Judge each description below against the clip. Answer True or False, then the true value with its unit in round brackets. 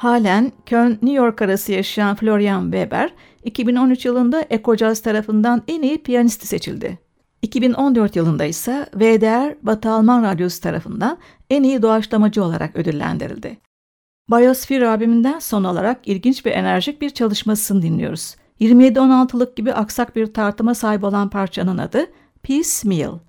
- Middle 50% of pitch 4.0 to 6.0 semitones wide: False (3.6 semitones)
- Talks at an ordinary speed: True (130 wpm)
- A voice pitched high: True (225 Hz)